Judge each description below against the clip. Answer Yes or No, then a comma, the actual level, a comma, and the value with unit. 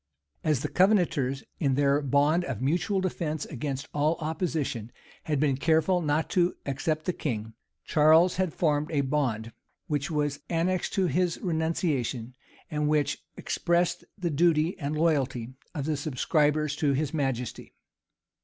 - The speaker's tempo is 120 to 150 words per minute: Yes, average, 145 wpm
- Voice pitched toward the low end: No, medium, 150 Hz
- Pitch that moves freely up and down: No, average, 3.1 semitones